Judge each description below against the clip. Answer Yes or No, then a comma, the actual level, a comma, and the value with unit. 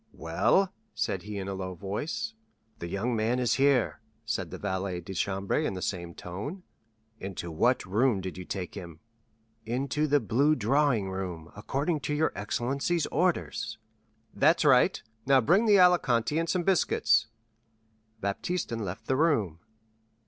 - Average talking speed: Yes, average, 150 wpm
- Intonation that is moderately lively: No, wide, 7.3 semitones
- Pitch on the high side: No, low, 115 Hz